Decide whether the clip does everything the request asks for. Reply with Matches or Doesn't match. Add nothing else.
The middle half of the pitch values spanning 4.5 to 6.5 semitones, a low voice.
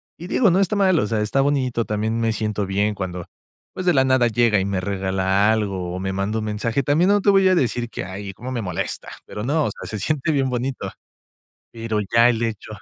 Matches